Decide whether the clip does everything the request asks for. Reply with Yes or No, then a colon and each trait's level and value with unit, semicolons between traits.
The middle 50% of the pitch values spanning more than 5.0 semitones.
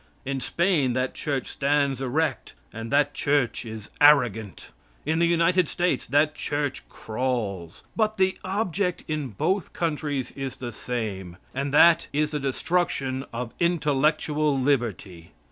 No: average, 4.6 semitones